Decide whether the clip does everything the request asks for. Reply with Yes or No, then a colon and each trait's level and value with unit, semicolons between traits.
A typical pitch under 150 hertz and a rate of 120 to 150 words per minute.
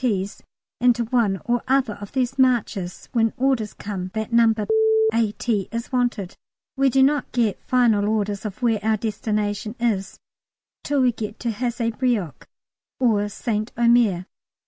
No: high, 230 Hz; average, 145 wpm